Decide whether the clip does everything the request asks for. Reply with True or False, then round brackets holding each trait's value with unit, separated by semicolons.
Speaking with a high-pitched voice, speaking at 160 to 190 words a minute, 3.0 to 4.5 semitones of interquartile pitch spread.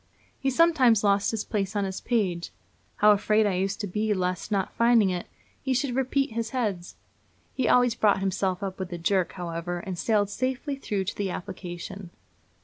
True (205 Hz; 185 wpm; 3.9 semitones)